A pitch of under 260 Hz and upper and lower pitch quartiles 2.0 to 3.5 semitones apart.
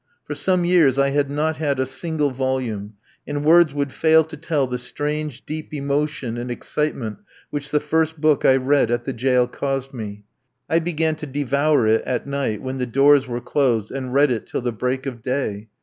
Yes: medium, 140 Hz; average, 3.1 semitones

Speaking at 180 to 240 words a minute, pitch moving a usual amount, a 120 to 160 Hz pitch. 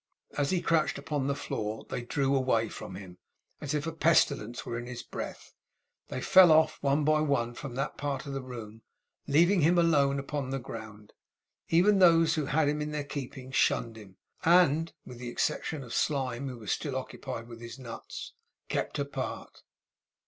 Yes: average, 185 wpm; average, 4.2 semitones; medium, 140 Hz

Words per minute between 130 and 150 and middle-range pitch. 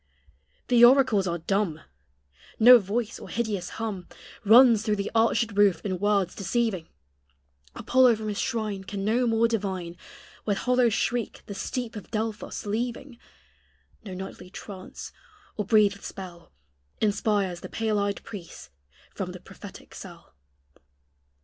No: slow, 135 wpm; high, 210 Hz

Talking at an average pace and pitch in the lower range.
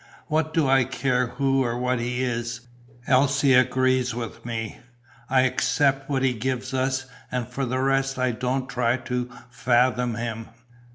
Yes: average, 160 wpm; low, 130 Hz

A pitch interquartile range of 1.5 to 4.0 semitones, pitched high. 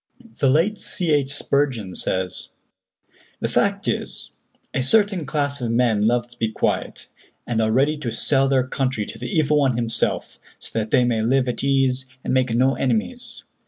No: average, 3.5 semitones; low, 130 Hz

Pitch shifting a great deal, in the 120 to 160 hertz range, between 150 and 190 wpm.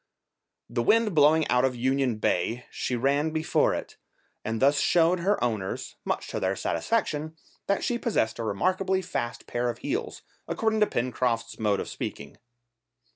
Yes: wide, 7.7 semitones; medium, 140 Hz; average, 160 wpm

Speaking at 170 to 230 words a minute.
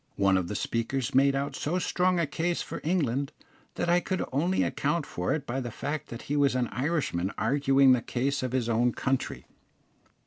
Yes: average, 200 wpm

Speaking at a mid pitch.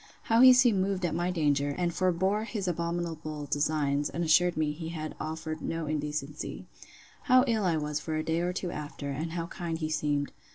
Yes: medium, 160 Hz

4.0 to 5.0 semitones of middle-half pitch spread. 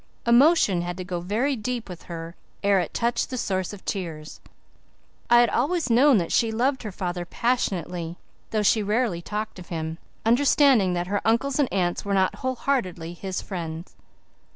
No: wide, 5.4 semitones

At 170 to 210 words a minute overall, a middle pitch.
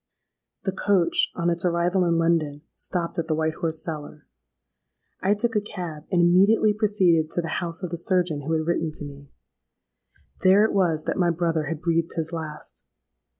Yes: average, 185 wpm; medium, 170 Hz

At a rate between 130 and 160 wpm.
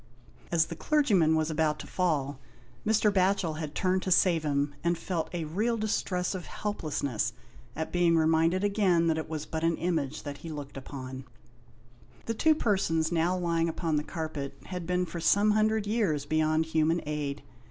No: average, 180 wpm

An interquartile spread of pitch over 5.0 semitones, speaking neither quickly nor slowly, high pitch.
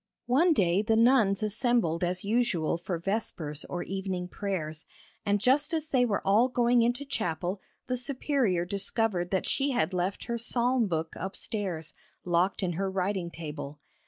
Yes: wide, 5.4 semitones; average, 160 wpm; high, 200 Hz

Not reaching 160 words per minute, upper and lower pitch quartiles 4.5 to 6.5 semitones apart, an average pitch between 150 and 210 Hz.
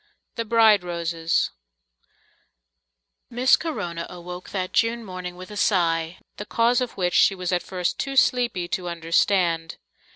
Yes: average, 140 wpm; average, 4.8 semitones; medium, 185 Hz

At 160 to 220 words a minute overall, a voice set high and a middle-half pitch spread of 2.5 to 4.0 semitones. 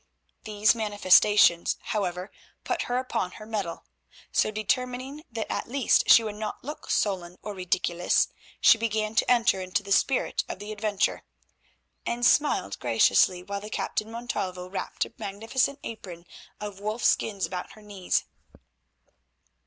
No: average, 145 wpm; high, 210 Hz; average, 3.4 semitones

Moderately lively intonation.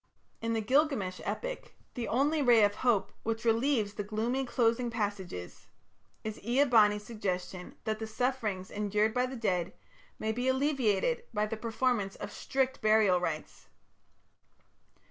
Yes: average, 3.5 semitones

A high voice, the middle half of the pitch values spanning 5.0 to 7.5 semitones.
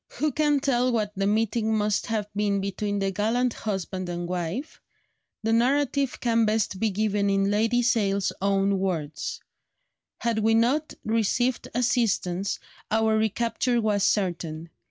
No: high, 215 Hz; average, 3.2 semitones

